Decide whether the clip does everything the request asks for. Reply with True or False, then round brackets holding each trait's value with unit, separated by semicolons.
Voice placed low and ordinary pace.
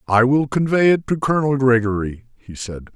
True (125 Hz; 185 wpm)